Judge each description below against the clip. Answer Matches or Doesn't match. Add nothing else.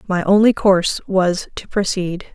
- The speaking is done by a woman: Matches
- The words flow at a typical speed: Matches